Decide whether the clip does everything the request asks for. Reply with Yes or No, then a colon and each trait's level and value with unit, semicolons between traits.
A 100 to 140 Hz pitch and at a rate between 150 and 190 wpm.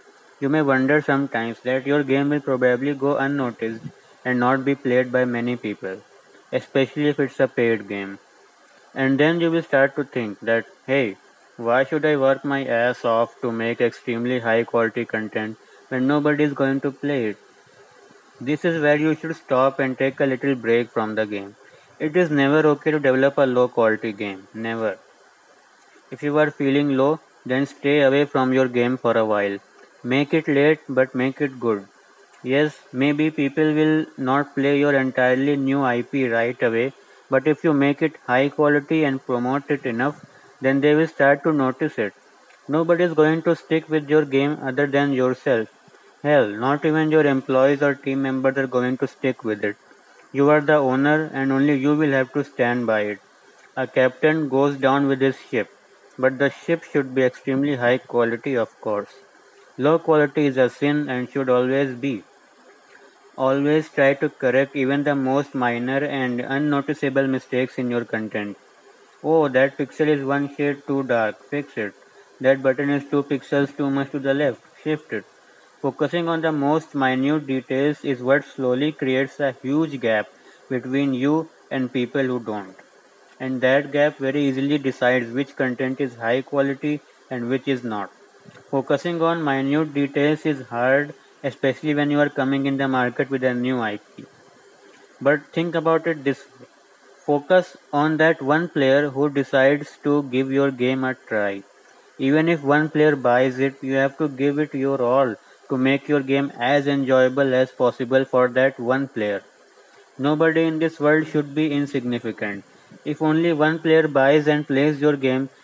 Yes: low, 135 Hz; average, 175 wpm